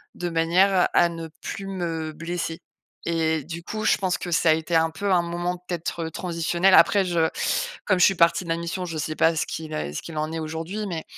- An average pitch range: No, narrow, 1.8 semitones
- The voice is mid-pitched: Yes, medium, 170 Hz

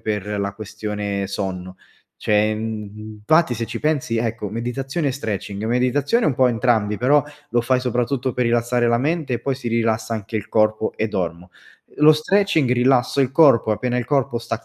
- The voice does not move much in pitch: No, average, 3.4 semitones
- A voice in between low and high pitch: No, low, 115 Hz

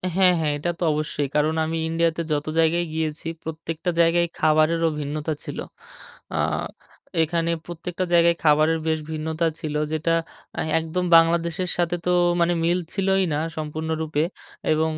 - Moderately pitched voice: Yes, medium, 160 Hz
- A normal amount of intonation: No, narrow, 1.6 semitones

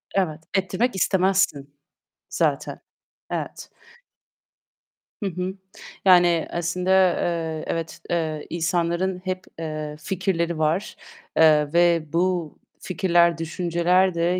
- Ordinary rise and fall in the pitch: No, narrow, 2.3 semitones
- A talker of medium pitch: Yes, medium, 170 Hz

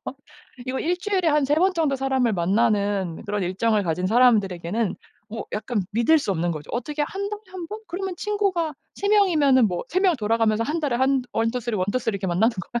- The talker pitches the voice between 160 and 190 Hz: No, high, 240 Hz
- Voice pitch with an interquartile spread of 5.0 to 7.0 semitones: No, wide, 7.8 semitones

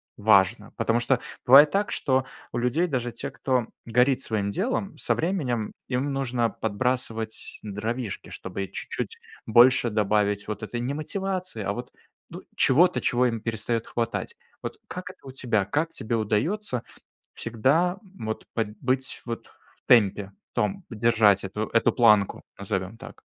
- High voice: No, low, 120 Hz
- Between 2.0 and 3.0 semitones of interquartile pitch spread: No, average, 3.7 semitones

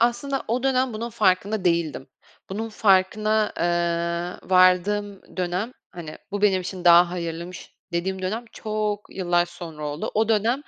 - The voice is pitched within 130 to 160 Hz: No, high, 190 Hz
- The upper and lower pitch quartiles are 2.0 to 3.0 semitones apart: No, average, 3.7 semitones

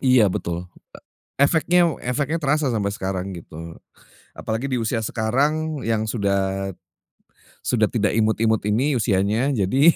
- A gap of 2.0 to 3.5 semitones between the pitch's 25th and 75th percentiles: No, wide, 5.6 semitones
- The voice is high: No, low, 110 Hz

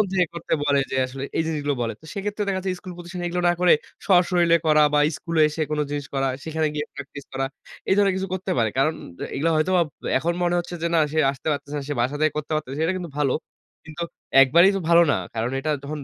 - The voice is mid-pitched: Yes, medium, 160 Hz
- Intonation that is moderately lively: Yes, average, 3.6 semitones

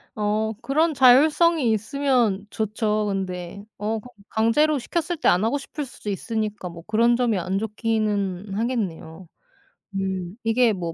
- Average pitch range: Yes, average, 4.2 semitones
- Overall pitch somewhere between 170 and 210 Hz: No, high, 220 Hz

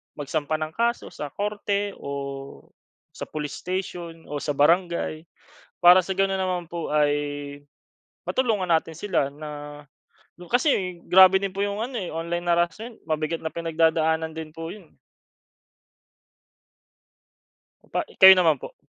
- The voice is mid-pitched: Yes, medium, 170 Hz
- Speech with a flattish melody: No, average, 3.4 semitones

